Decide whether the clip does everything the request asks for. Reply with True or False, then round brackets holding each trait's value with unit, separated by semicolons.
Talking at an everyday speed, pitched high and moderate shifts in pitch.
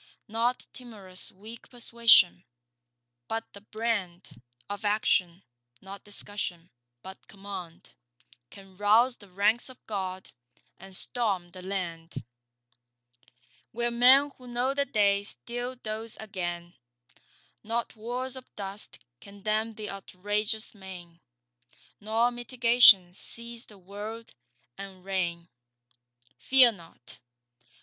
False (105 wpm; 205 Hz; 3.8 semitones)